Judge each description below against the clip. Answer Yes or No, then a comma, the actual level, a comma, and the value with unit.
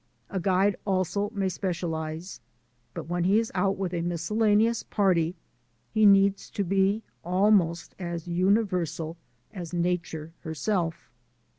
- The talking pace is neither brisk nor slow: No, slow, 125 wpm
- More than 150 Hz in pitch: Yes, medium, 185 Hz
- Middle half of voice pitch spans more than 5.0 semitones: No, average, 2.9 semitones